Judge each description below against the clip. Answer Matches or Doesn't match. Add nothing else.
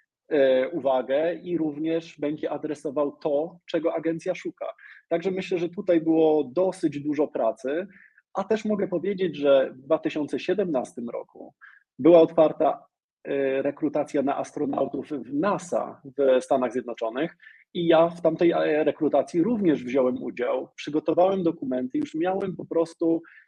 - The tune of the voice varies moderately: Matches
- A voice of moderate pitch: Matches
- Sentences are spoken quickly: Doesn't match